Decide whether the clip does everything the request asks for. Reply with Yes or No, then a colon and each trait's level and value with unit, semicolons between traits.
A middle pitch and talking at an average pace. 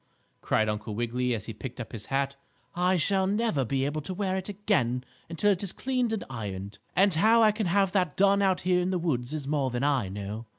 No: medium, 155 Hz; fast, 230 wpm